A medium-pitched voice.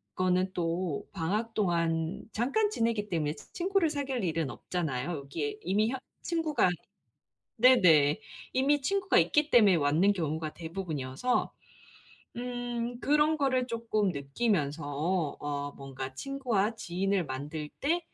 No: high, 195 Hz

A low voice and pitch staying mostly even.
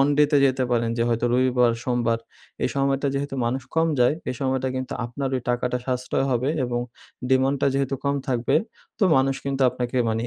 Yes: low, 130 Hz; narrow, 2.0 semitones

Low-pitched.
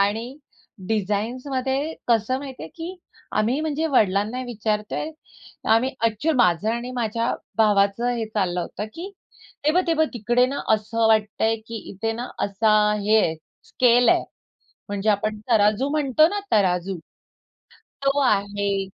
No: high, 225 Hz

